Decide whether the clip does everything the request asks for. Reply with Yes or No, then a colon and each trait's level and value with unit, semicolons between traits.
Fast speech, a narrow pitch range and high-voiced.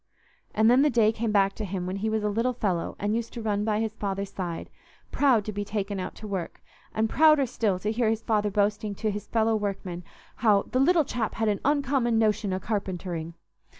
Yes: fast, 220 wpm; narrow, 2.3 semitones; high, 215 Hz